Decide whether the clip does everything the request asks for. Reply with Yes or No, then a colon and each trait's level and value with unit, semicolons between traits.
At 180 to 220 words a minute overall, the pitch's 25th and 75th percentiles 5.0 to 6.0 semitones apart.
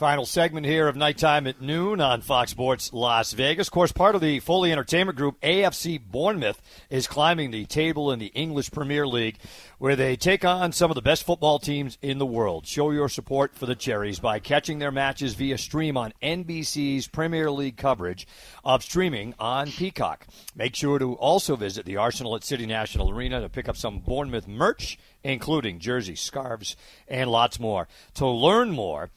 No: average, 185 wpm; average, 4.4 semitones